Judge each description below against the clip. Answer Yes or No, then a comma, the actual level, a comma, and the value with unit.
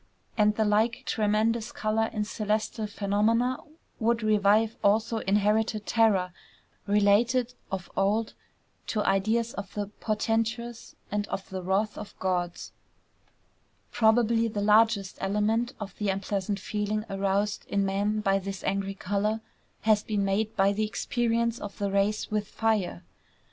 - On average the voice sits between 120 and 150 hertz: No, high, 210 Hz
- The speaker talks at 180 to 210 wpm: No, slow, 135 wpm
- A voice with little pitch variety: Yes, narrow, 2.0 semitones